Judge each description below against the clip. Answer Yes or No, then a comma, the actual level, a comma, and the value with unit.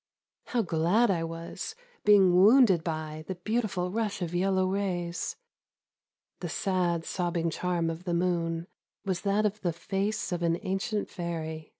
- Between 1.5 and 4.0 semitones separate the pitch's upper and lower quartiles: Yes, average, 2.8 semitones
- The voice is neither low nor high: Yes, medium, 180 Hz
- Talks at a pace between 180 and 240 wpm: No, average, 150 wpm